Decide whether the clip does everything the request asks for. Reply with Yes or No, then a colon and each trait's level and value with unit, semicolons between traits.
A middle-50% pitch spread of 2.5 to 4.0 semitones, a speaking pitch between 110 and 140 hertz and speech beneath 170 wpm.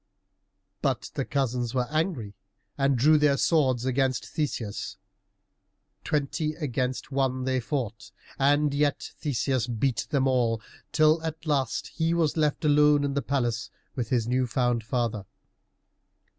Yes: average, 3.4 semitones; low, 135 Hz; slow, 135 wpm